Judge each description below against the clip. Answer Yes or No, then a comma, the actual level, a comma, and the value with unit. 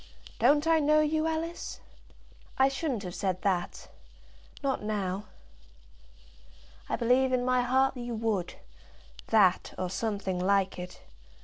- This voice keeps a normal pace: No, slow, 125 wpm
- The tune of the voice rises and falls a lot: Yes, wide, 6.0 semitones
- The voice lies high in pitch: Yes, high, 235 Hz